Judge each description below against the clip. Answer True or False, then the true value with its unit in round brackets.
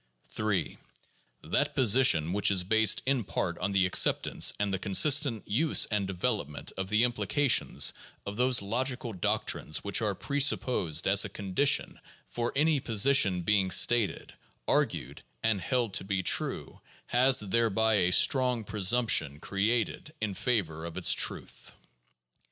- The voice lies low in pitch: True (105 Hz)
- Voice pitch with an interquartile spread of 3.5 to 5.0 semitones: True (4.4 semitones)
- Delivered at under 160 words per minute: True (145 wpm)